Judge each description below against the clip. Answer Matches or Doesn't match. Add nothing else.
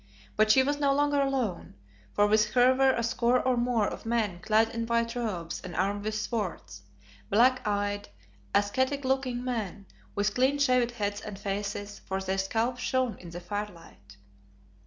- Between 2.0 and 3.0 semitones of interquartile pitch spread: Doesn't match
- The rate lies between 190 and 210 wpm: Doesn't match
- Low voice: Doesn't match